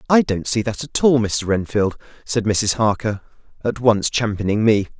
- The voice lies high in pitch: No, low, 110 Hz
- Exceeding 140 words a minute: Yes, average, 180 wpm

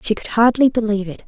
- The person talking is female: Yes, female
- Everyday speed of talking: No, fast, 235 wpm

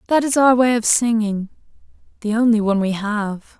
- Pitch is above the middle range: Yes, high, 225 Hz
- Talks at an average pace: Yes, average, 185 wpm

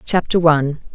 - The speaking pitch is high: No, medium, 160 Hz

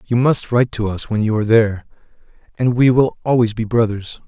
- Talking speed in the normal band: No, fast, 210 wpm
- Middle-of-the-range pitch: No, low, 115 Hz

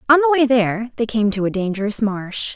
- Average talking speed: No, fast, 235 wpm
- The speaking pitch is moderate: No, high, 230 Hz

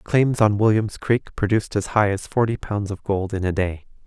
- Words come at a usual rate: No, fast, 220 wpm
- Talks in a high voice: No, low, 105 Hz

